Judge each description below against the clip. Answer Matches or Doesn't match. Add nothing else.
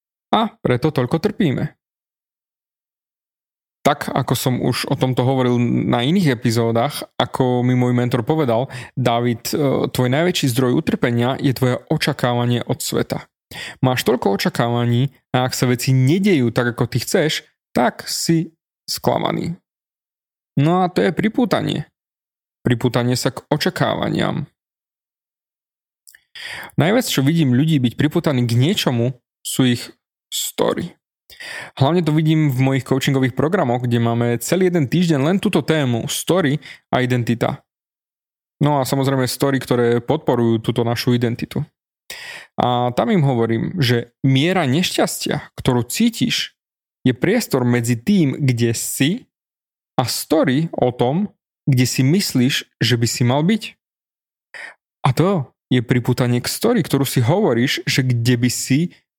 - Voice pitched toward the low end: Matches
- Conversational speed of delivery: Matches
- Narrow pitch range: Doesn't match